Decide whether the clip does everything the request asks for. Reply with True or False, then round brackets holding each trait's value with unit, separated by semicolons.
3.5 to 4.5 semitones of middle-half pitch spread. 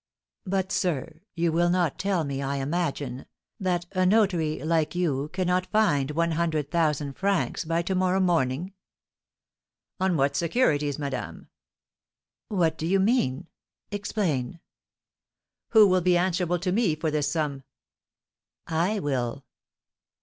True (3.9 semitones)